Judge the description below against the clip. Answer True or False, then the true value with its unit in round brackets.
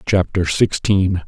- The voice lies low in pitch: True (90 Hz)